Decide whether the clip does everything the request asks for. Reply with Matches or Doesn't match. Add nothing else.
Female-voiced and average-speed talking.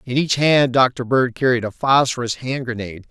Doesn't match